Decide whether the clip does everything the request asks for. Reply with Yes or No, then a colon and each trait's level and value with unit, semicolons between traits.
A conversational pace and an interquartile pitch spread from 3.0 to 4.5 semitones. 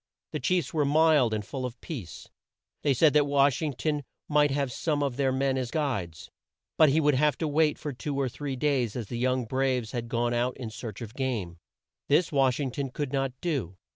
No: fast, 220 wpm; average, 3.3 semitones